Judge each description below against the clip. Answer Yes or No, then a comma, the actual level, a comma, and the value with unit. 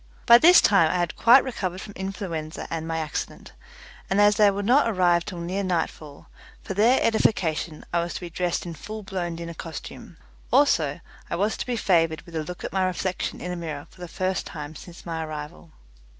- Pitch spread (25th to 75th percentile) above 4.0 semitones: No, average, 3.4 semitones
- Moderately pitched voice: Yes, medium, 175 Hz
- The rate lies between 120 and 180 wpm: No, fast, 205 wpm